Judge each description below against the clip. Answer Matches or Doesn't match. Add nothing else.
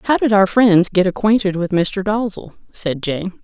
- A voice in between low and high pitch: Doesn't match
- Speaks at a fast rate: Doesn't match